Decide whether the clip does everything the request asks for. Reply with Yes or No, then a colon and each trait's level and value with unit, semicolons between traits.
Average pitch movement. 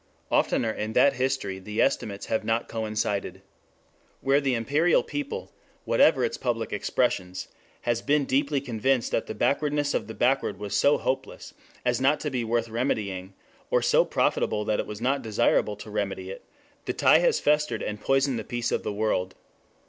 Yes: average, 4.3 semitones